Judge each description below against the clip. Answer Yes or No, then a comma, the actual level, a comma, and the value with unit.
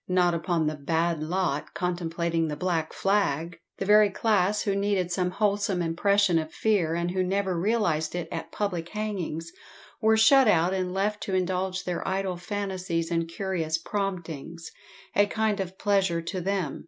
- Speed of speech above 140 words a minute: Yes, average, 165 wpm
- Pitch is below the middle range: No, medium, 185 Hz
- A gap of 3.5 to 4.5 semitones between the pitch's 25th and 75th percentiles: No, average, 3.0 semitones